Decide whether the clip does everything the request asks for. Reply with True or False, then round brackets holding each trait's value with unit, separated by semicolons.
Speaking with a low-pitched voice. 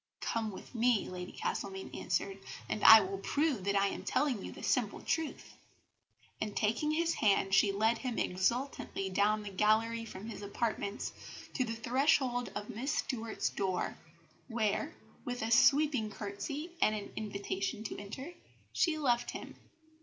False (220 Hz)